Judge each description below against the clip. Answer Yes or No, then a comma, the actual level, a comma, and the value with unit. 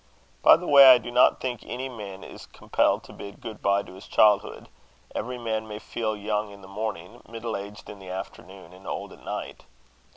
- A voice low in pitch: Yes, low, 105 Hz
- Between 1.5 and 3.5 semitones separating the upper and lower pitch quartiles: Yes, average, 2.9 semitones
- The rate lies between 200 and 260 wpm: Yes, fast, 205 wpm